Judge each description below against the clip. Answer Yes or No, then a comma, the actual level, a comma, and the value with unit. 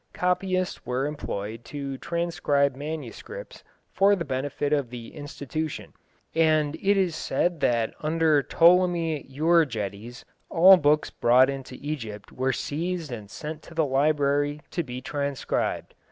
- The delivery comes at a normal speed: No, slow, 130 wpm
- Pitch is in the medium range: Yes, medium, 145 Hz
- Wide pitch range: No, average, 3.9 semitones